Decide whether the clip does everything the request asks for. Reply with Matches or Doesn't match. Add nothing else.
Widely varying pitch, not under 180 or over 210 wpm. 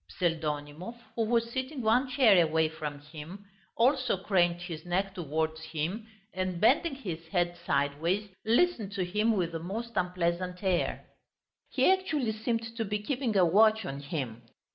Doesn't match